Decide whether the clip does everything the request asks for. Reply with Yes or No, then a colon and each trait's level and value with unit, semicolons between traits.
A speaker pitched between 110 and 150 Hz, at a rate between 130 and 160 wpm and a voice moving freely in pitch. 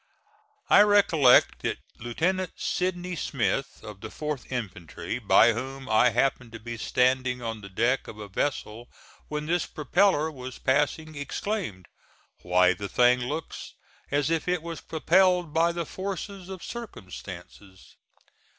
Yes: low, 135 Hz; average, 140 wpm; wide, 6.9 semitones